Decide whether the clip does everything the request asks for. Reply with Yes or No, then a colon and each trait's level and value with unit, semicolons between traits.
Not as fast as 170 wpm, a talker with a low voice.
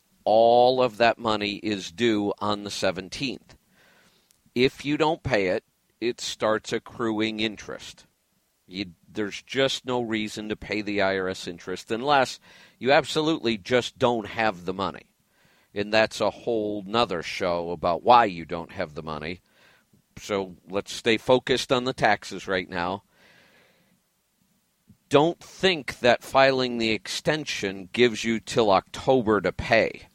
Yes: average, 140 wpm; low, 110 Hz